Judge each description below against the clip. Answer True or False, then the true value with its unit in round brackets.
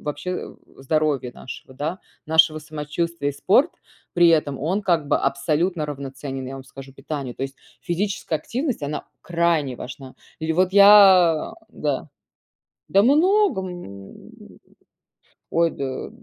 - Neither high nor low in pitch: True (155 Hz)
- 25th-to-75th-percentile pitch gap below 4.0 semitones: False (4.8 semitones)